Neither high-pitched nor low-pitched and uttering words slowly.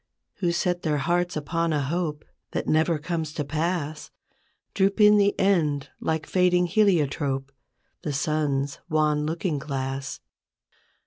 Yes: medium, 155 Hz; slow, 130 wpm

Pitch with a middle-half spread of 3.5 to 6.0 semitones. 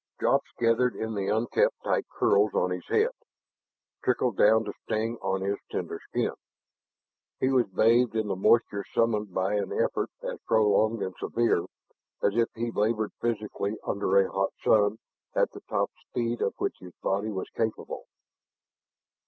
No: narrow, 2.6 semitones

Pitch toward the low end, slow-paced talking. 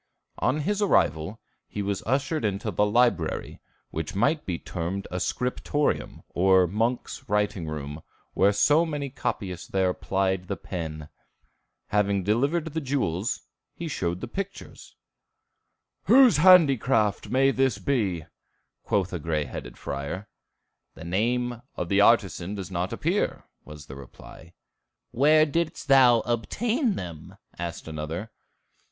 Yes: low, 105 Hz; slow, 130 wpm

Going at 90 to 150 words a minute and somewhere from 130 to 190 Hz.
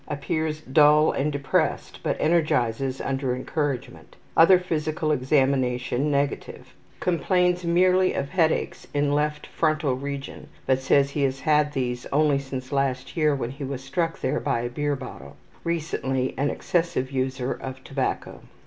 Yes: average, 145 wpm; medium, 140 Hz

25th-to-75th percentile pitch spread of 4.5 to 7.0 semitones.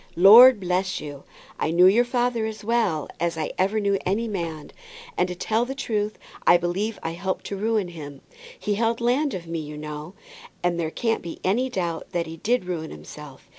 Yes: average, 5.1 semitones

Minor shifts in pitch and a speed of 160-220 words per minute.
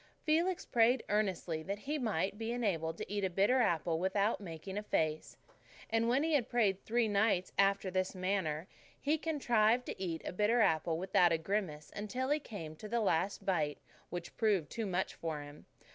No: average, 5.0 semitones; average, 190 wpm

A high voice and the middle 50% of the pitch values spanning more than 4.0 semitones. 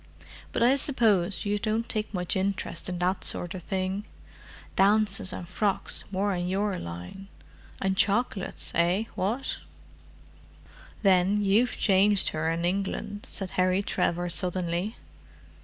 No: high, 195 Hz; narrow, 2.4 semitones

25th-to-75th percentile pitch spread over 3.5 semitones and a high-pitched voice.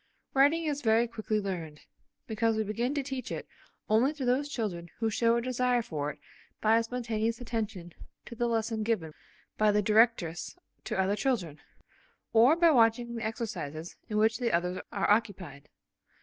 No: average, 3.0 semitones; high, 225 Hz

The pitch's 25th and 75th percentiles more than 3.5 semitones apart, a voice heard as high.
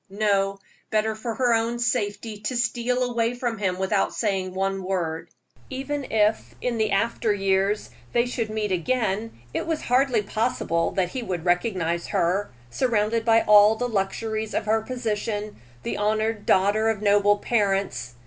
No: average, 3.0 semitones; high, 215 Hz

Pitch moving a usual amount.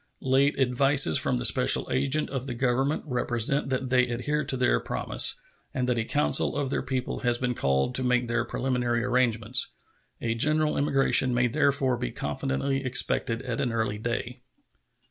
No: narrow, 2.3 semitones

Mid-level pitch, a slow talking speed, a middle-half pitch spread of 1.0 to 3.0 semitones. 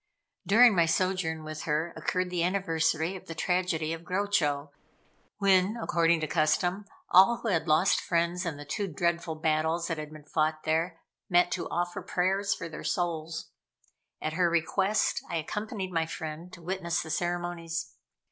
No: medium, 170 Hz; average, 165 wpm; narrow, 2.5 semitones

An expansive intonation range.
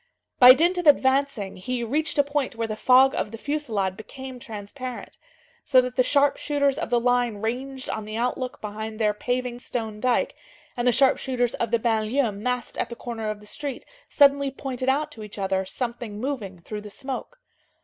No: average, 3.7 semitones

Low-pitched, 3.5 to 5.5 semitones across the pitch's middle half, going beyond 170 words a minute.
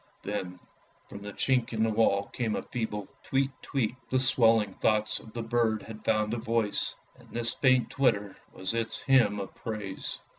No: low, 110 Hz; narrow, 2.4 semitones; average, 180 wpm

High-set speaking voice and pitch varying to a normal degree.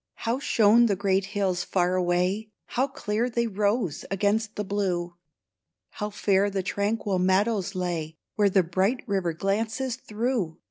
Yes: high, 200 Hz; average, 3.0 semitones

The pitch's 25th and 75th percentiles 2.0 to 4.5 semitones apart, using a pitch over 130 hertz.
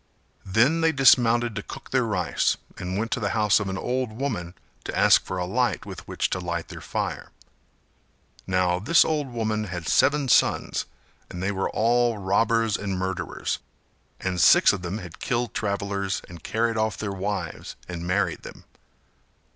No: average, 4.2 semitones; low, 105 Hz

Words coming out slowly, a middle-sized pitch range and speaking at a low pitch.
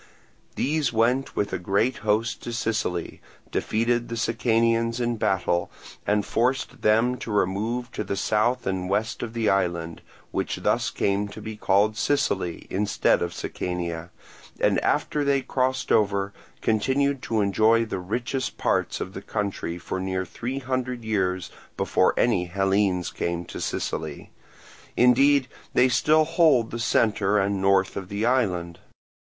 No: average, 150 wpm; average, 4.0 semitones; low, 110 Hz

